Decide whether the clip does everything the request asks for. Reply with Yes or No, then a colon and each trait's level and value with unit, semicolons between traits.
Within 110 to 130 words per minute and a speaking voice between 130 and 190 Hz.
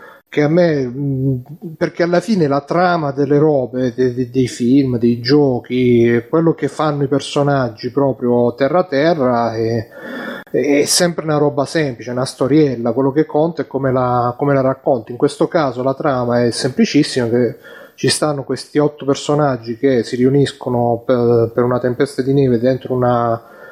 No: average, 160 wpm; low, 135 Hz